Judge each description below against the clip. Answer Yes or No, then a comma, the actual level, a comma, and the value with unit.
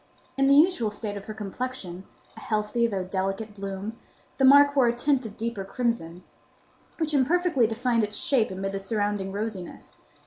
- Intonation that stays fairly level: No, average, 4.6 semitones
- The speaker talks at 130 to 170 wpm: Yes, average, 160 wpm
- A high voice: Yes, high, 220 Hz